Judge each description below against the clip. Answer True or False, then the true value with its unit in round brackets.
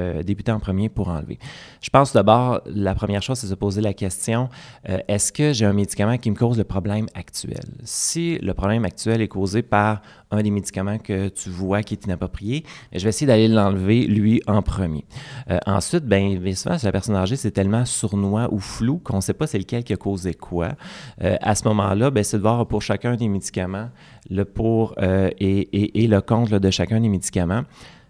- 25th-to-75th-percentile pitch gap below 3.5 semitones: True (2.8 semitones)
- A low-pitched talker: True (105 Hz)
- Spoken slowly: False (215 wpm)